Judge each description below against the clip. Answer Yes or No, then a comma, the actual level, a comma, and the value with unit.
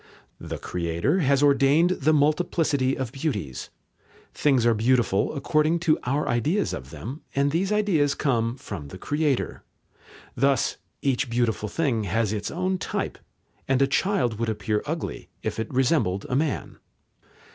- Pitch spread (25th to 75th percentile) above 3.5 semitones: Yes, average, 5.2 semitones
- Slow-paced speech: No, average, 145 wpm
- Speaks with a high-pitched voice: No, low, 135 Hz